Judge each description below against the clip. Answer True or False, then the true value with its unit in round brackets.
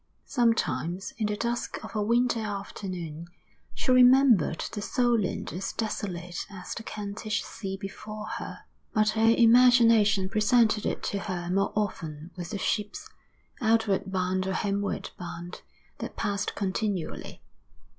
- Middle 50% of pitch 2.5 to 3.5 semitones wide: True (3.2 semitones)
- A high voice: True (205 Hz)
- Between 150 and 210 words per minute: False (135 wpm)